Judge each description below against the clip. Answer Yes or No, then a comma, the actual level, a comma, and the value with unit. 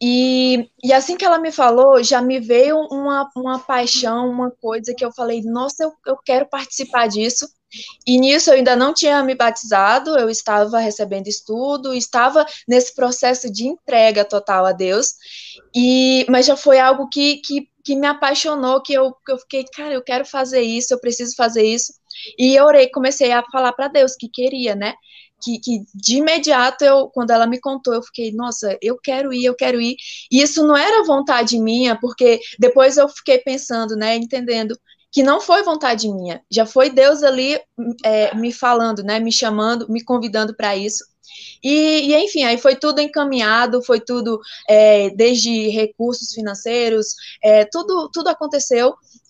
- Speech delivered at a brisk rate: No, average, 175 wpm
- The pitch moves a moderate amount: Yes, average, 3.0 semitones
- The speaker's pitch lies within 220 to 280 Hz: Yes, very high, 250 Hz